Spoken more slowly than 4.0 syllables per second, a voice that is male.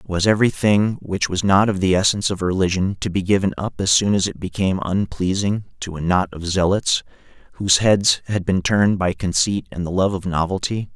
No: 5.5 syllables/s; male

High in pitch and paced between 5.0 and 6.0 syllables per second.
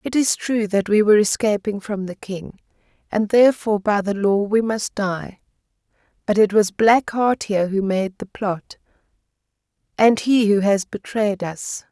No: high, 205 Hz; 4.6 syllables/s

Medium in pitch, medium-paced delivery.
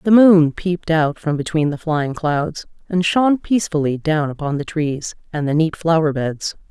Yes: medium, 160 Hz; average, 190 wpm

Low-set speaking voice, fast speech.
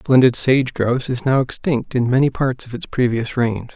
Yes: low, 125 Hz; fast, 225 wpm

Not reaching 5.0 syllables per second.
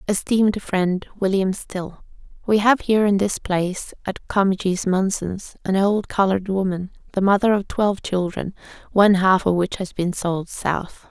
Yes: 4.8 syllables/s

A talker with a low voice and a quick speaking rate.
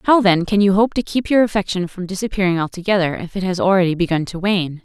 No: medium, 185 Hz; fast, 235 wpm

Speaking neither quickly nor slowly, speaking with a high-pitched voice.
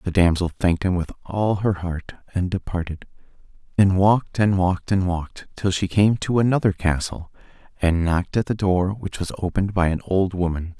No: average, 190 wpm; very low, 95 Hz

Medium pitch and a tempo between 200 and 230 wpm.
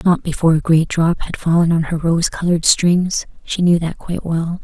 Yes: medium, 170 Hz; fast, 205 wpm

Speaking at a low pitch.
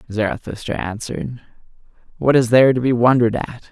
Yes: low, 120 Hz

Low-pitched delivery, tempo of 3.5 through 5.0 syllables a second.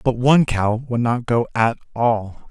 Yes: low, 120 Hz; 4.2 syllables/s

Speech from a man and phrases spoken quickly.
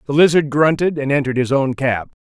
Yes: male; fast, 215 wpm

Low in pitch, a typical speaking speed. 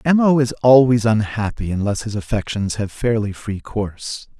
Yes: low, 110 Hz; average, 165 wpm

